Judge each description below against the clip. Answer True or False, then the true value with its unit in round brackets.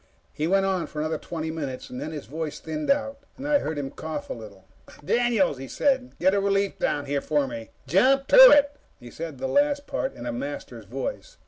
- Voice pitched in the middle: True (160 Hz)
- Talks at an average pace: False (215 wpm)